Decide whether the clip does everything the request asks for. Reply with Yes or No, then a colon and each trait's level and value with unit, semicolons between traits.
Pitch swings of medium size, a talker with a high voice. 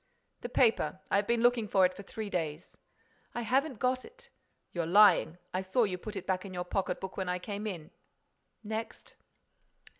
Yes: average, 4.1 semitones; high, 200 Hz